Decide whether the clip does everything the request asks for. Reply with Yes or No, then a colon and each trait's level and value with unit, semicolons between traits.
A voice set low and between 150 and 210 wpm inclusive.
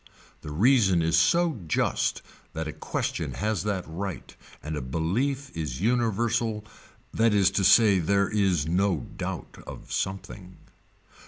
No: low, 100 Hz; average, 140 wpm